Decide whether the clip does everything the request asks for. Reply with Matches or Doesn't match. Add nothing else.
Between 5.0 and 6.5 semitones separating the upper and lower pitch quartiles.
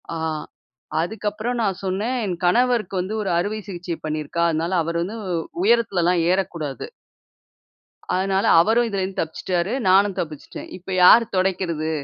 Doesn't match